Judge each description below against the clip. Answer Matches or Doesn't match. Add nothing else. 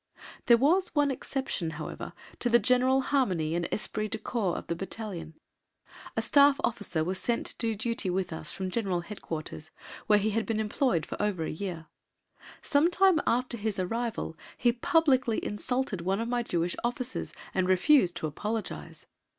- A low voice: Doesn't match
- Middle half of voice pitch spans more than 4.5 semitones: Matches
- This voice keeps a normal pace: Matches